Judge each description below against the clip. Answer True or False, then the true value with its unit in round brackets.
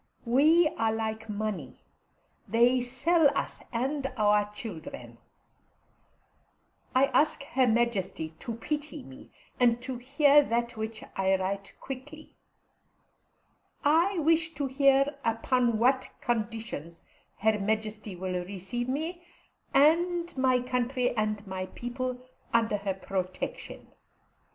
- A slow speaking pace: True (110 wpm)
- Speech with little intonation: False (4.5 semitones)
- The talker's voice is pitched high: True (240 Hz)